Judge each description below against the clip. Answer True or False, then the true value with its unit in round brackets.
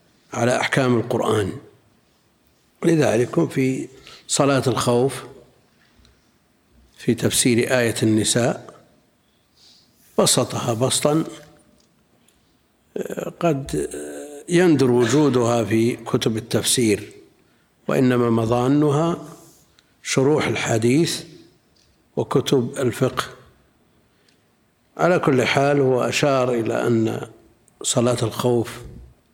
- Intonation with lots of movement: False (3.0 semitones)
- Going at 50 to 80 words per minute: True (70 wpm)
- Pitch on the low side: True (125 Hz)